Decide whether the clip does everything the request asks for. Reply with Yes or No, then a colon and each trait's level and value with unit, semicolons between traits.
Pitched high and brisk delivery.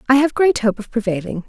Yes: high, 240 Hz; fast, 245 wpm